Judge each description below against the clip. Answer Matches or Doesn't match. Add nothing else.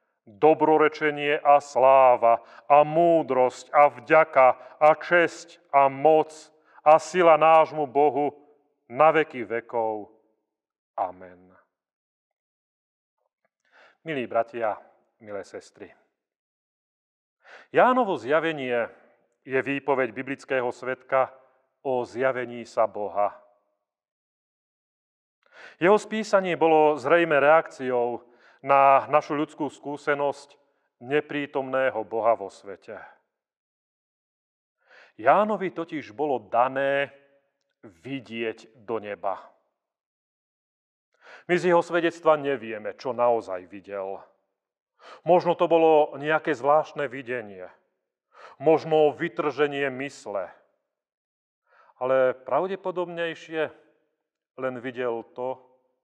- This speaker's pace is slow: Matches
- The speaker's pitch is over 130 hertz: Matches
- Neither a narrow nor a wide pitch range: Matches